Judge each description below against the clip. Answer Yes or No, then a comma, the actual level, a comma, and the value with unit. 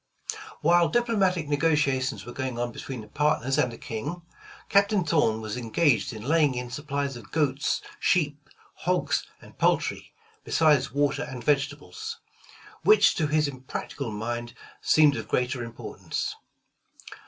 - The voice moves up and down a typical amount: Yes, average, 4.3 semitones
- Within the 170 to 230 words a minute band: No, slow, 135 wpm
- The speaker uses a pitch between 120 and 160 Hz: Yes, medium, 140 Hz